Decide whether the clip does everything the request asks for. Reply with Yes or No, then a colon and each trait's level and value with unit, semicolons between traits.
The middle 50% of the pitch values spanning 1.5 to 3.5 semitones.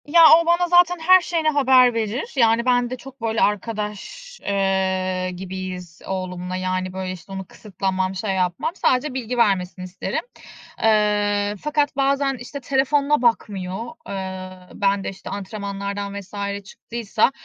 No: wide, 5.5 semitones